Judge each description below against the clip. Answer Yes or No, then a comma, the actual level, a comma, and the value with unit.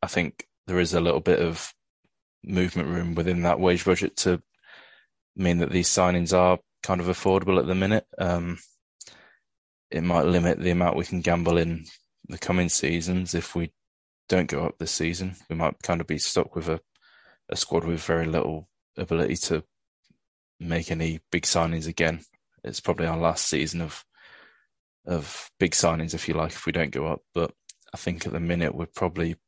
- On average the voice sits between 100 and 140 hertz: No, very low, 85 Hz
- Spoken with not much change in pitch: Yes, narrow, 1.5 semitones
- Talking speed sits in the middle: Yes, average, 185 wpm